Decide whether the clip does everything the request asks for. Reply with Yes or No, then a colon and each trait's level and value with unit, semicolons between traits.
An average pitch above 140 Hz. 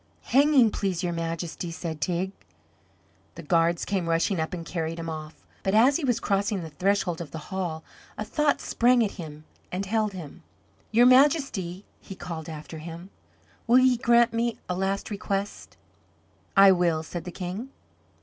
Yes: medium, 185 Hz